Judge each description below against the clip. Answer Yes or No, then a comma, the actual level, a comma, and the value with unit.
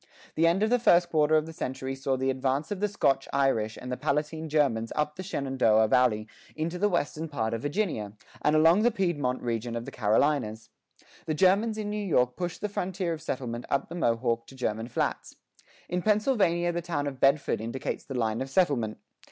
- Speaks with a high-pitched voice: No, medium, 145 Hz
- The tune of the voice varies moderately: No, wide, 5.8 semitones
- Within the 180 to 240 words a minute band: Yes, average, 200 wpm